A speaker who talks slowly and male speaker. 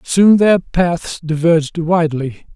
Yes: slow, 120 wpm; male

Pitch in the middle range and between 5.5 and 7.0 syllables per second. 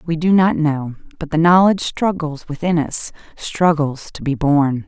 No: medium, 155 Hz; 4.4 syllables/s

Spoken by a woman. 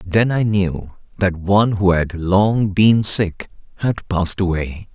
No: male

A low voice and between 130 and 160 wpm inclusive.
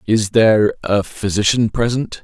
Yes: low, 110 Hz; slow, 135 wpm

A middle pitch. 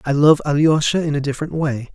Yes: medium, 145 Hz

